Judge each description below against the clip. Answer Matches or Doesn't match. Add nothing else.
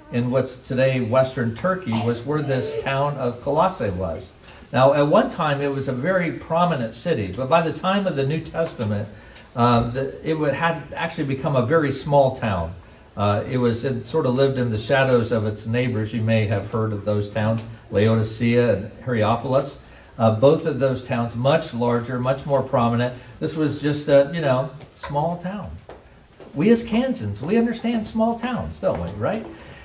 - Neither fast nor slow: Matches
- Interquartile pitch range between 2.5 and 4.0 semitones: Doesn't match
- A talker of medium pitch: Doesn't match